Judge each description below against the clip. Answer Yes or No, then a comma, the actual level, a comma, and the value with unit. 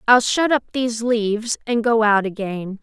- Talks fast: No, average, 190 wpm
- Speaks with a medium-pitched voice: No, high, 225 Hz